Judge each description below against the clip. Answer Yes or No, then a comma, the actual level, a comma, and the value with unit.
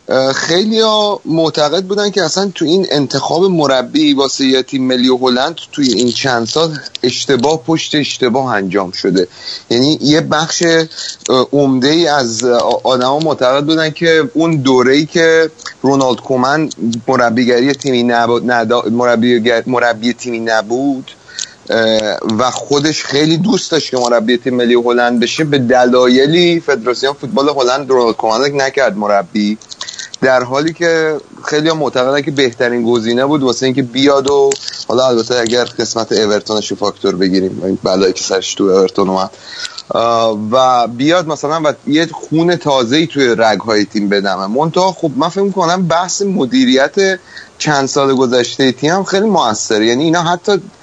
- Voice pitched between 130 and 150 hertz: Yes, low, 135 Hz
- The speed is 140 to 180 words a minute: Yes, average, 145 wpm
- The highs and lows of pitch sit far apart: No, average, 4.7 semitones